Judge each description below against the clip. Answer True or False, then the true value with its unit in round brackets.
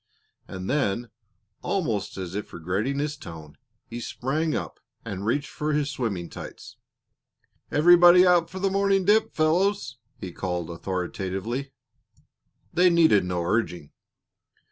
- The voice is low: True (130 Hz)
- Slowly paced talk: True (125 wpm)